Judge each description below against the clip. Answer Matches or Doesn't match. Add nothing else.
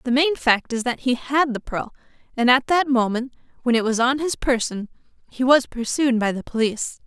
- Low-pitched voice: Doesn't match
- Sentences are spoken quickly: Matches